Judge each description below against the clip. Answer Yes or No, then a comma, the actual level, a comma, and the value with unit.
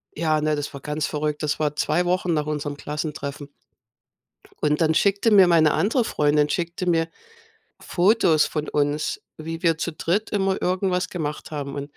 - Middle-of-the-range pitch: Yes, medium, 155 Hz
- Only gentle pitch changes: No, average, 3.1 semitones